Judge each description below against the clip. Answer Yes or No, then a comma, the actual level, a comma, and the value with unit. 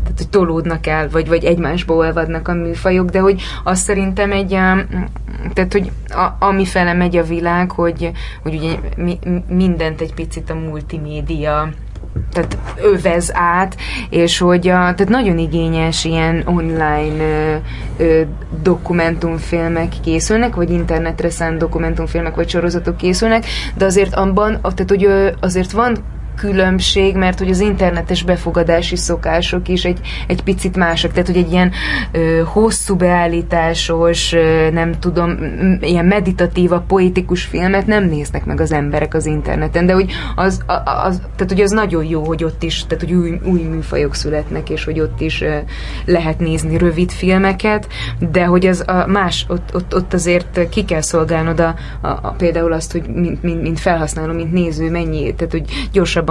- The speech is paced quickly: Yes, fast, 160 wpm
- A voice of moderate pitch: Yes, medium, 170 Hz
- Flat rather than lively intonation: Yes, narrow, 2.1 semitones